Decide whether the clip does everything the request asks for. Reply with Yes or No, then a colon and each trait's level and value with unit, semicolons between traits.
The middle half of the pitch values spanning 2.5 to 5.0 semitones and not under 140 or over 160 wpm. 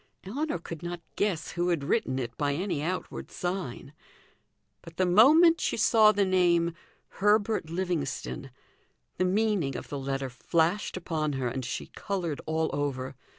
No: wide, 5.5 semitones; average, 150 wpm